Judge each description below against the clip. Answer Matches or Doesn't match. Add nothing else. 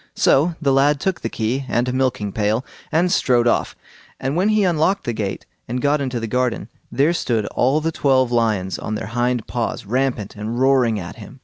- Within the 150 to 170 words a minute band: Doesn't match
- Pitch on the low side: Matches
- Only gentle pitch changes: Doesn't match